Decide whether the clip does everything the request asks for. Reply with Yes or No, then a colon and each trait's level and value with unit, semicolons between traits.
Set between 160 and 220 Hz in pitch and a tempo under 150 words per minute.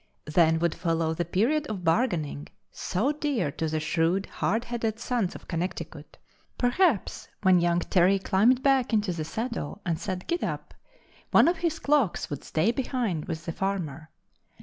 No: high, 190 Hz; average, 165 wpm